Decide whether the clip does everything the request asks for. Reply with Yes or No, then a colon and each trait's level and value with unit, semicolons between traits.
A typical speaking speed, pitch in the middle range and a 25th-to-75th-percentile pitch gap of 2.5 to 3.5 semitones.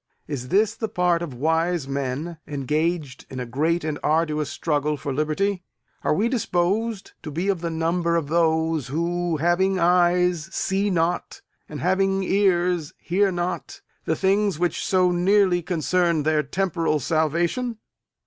Yes: average, 150 wpm; medium, 170 Hz; average, 3.1 semitones